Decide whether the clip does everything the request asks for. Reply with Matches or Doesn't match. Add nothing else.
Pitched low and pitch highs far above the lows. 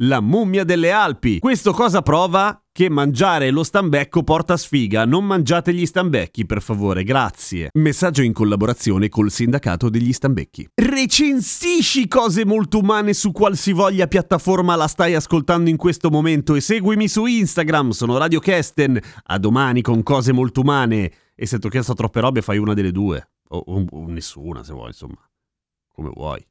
Doesn't match